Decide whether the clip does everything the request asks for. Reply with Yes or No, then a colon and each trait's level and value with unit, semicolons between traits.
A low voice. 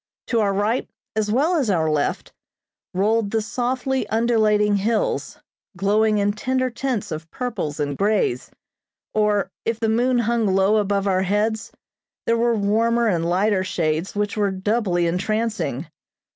No: high, 210 Hz